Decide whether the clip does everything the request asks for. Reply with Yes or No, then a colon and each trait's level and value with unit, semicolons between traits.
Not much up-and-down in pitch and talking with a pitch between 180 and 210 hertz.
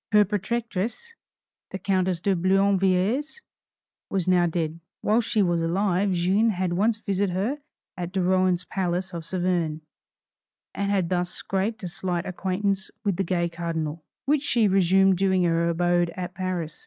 Yes: narrow, 2.3 semitones; medium, 185 Hz